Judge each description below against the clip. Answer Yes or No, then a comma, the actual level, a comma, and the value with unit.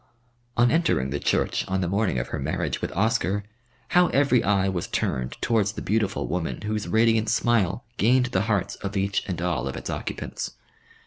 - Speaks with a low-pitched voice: Yes, low, 100 Hz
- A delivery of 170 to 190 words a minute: Yes, average, 185 wpm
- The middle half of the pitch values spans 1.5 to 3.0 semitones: No, average, 3.5 semitones